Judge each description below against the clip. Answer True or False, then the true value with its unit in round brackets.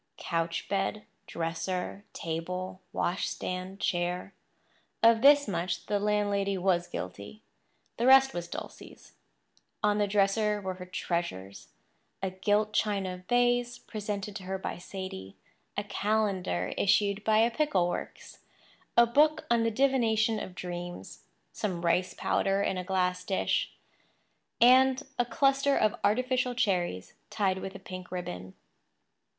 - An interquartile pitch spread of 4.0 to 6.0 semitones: False (3.4 semitones)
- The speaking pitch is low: False (195 Hz)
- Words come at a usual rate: False (125 wpm)